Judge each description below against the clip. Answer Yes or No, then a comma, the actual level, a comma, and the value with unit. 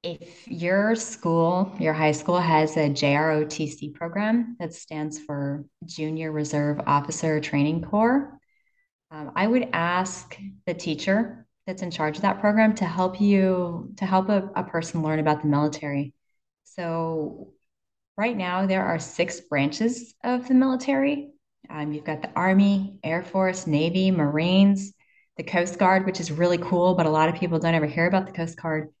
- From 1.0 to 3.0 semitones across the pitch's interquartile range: No, average, 4.1 semitones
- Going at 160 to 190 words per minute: Yes, average, 165 wpm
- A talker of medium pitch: Yes, medium, 175 Hz